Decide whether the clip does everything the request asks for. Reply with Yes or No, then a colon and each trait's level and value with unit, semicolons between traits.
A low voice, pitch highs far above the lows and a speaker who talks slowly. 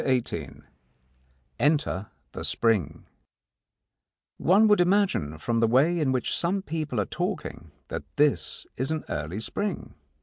Yes: low, 130 Hz; wide, 8.3 semitones; slow, 130 wpm